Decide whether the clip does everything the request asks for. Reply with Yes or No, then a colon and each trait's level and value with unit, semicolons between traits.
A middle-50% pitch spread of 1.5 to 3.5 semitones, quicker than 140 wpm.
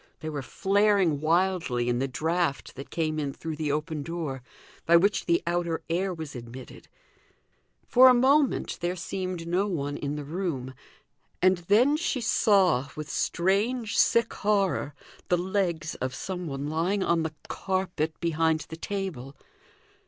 No: average, 4.2 semitones; average, 150 wpm